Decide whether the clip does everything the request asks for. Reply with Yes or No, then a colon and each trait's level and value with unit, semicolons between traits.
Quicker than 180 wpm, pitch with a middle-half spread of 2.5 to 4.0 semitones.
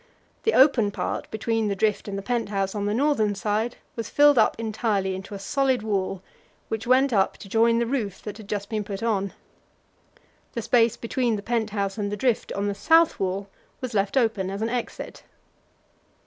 Yes: average, 200 wpm; average, 2.9 semitones